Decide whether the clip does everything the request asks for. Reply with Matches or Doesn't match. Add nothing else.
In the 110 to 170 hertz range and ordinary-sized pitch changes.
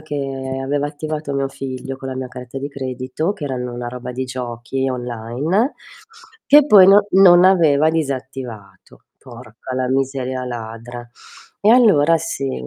Matches